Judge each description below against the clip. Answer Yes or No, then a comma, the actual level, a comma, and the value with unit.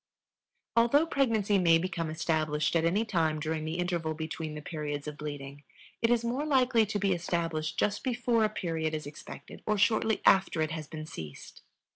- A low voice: No, medium, 170 Hz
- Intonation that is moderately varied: No, wide, 5.8 semitones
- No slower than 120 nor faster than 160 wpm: No, average, 175 wpm